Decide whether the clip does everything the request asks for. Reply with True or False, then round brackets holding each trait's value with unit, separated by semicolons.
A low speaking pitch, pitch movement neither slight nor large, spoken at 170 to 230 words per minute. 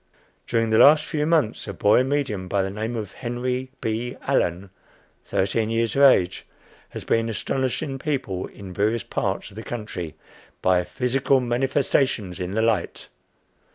False (115 Hz; 4.8 semitones; 155 wpm)